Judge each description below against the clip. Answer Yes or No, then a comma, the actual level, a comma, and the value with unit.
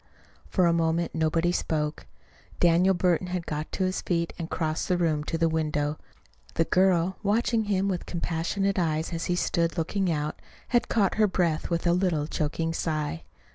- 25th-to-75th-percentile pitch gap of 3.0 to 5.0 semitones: No, narrow, 2.5 semitones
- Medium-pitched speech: Yes, medium, 170 Hz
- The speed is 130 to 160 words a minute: No, average, 175 wpm